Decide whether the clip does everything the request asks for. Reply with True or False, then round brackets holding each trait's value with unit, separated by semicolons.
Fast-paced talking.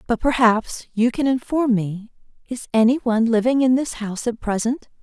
False (165 wpm)